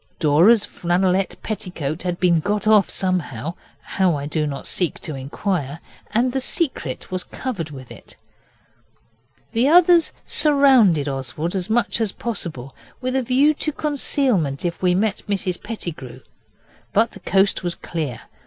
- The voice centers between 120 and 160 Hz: No, medium, 185 Hz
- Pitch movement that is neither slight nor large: No, wide, 6.8 semitones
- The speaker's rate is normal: Yes, average, 145 wpm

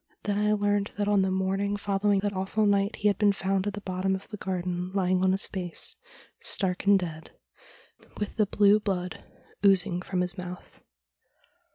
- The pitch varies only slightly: Yes, narrow, 1.8 semitones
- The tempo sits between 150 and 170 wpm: No, average, 185 wpm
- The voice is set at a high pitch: Yes, high, 195 Hz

